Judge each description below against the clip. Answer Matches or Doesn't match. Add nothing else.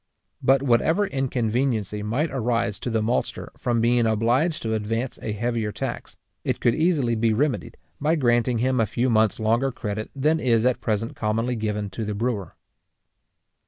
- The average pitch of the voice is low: Matches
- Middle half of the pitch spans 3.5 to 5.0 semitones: Doesn't match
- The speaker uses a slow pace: Doesn't match